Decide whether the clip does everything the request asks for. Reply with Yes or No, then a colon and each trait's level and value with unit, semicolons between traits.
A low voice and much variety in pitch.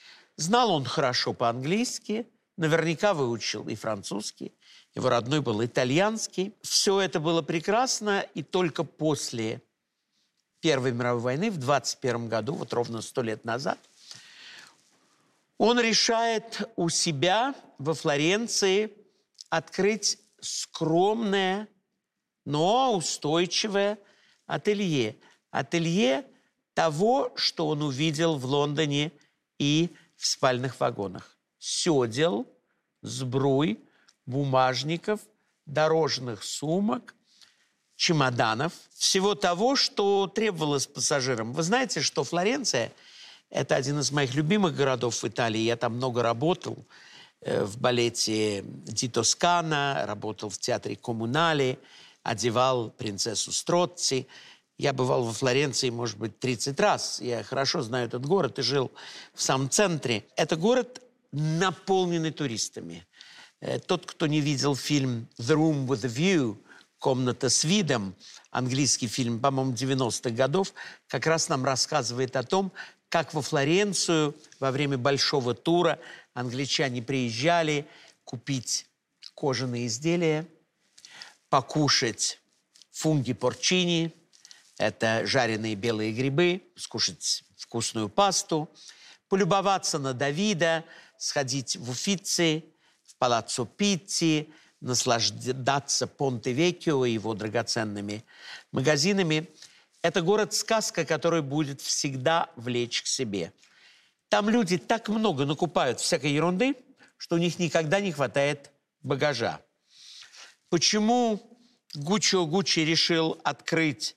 No: medium, 155 Hz; wide, 6.3 semitones